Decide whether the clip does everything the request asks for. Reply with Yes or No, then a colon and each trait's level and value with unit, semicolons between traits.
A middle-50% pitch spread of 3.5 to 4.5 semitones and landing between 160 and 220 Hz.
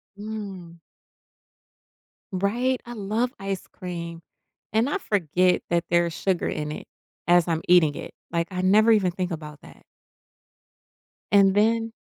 Yes: average, 3.9 semitones; medium, 185 Hz